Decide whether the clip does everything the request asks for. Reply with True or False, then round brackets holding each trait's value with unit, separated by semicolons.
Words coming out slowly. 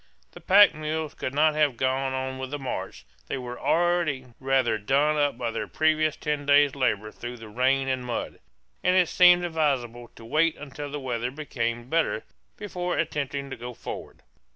False (175 wpm)